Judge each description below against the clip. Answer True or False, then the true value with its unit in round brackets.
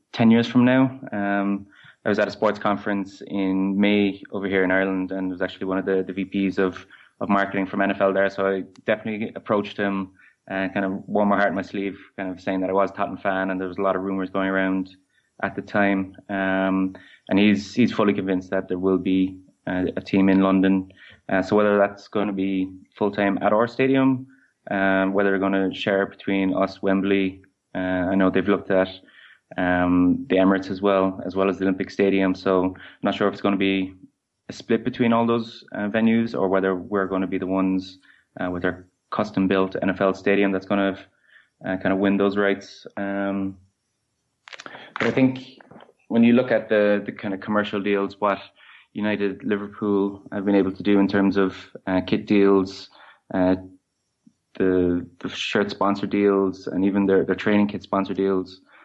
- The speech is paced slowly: False (205 wpm)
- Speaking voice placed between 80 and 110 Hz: True (95 Hz)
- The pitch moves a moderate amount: False (1.1 semitones)